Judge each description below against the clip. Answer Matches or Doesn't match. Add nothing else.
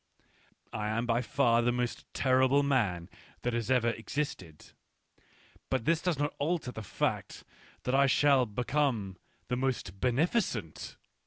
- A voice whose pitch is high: Doesn't match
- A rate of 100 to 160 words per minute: Matches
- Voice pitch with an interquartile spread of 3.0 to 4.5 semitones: Matches